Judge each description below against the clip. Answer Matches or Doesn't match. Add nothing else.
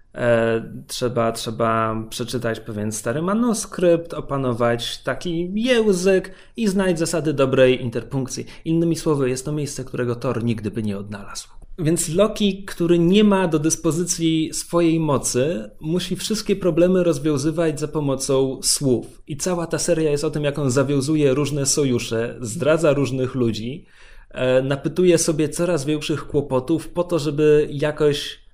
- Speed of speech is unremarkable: Matches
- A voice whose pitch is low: Doesn't match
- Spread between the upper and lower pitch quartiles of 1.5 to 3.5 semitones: Doesn't match